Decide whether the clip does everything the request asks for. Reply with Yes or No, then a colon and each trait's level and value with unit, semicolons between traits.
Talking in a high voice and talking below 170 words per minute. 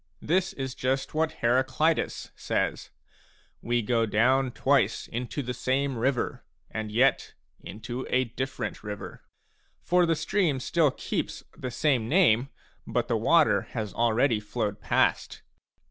No: low, 130 Hz; average, 140 wpm